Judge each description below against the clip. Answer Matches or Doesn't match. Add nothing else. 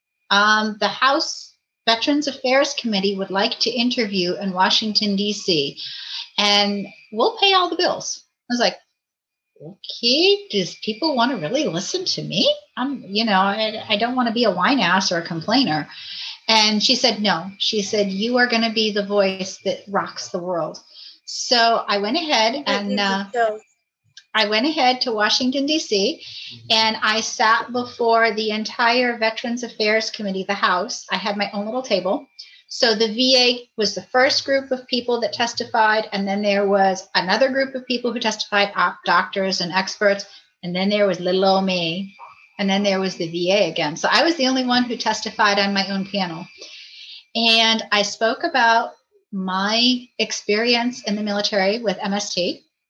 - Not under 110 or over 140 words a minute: Doesn't match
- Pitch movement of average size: Matches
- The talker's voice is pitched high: Matches